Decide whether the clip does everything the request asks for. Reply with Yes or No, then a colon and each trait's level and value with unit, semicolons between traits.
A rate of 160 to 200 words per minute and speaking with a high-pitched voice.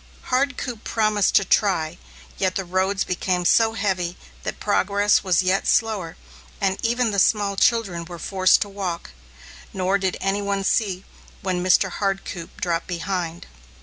No: average, 150 wpm; high, 195 Hz